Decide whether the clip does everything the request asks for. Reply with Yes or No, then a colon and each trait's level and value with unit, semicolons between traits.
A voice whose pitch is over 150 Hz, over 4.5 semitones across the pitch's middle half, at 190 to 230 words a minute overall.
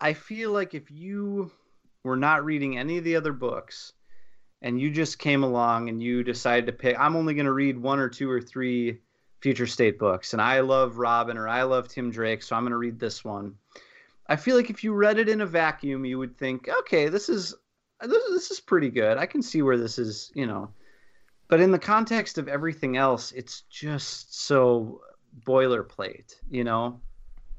No: low, 130 Hz; average, 5.0 semitones; average, 200 wpm